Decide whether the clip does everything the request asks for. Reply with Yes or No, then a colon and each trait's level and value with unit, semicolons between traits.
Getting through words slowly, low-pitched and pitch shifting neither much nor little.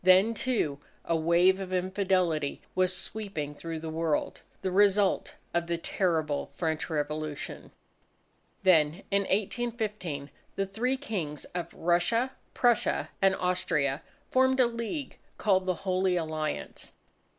No: slow, 125 wpm; medium, 185 Hz; average, 4.1 semitones